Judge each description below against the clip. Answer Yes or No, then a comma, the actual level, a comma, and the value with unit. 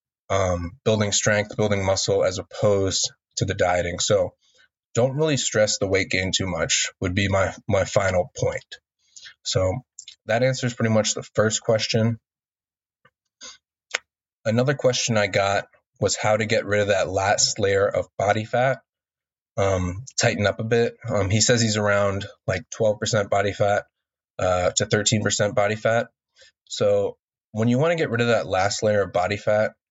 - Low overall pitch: Yes, low, 105 Hz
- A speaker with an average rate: Yes, average, 165 wpm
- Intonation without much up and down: No, average, 3.0 semitones